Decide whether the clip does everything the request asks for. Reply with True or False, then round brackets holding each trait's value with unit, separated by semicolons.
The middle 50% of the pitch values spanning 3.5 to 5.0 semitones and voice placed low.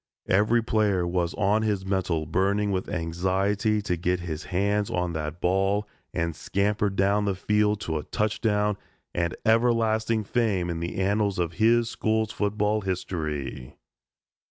False (3.1 semitones; 100 Hz)